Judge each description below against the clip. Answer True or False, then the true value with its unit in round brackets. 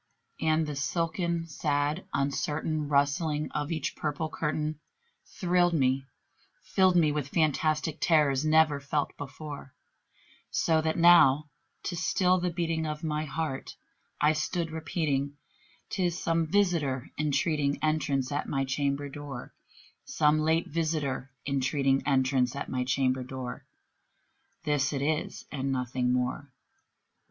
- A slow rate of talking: True (125 wpm)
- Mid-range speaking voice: True (150 Hz)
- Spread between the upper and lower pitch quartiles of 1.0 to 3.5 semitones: True (2.6 semitones)